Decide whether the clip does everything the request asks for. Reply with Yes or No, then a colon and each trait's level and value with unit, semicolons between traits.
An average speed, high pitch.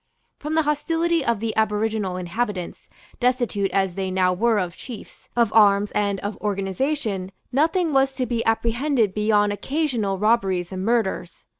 Yes: average, 150 wpm; high, 220 Hz